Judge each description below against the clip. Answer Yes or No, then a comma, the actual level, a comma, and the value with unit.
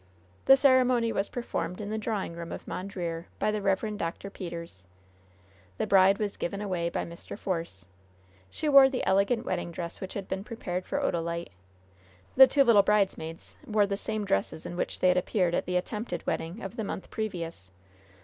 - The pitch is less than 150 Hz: No, high, 195 Hz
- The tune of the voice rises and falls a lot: No, average, 4.0 semitones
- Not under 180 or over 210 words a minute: Yes, average, 185 wpm